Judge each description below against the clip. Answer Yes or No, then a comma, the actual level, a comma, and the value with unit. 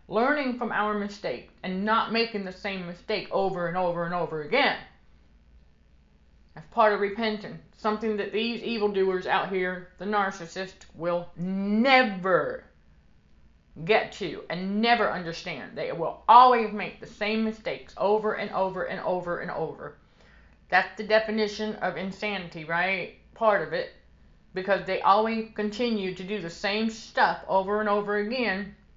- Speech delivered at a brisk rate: No, average, 145 wpm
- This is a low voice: No, high, 195 Hz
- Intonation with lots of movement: No, average, 3.6 semitones